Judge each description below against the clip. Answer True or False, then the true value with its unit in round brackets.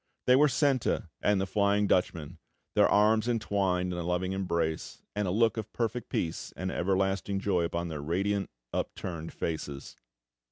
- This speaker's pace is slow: False (160 wpm)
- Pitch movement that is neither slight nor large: True (3.2 semitones)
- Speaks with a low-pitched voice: True (95 Hz)